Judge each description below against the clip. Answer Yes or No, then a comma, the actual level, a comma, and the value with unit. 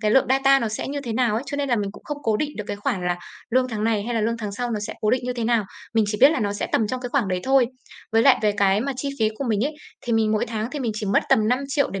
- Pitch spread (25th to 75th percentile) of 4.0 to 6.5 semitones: No, average, 3.5 semitones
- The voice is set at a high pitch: Yes, high, 230 Hz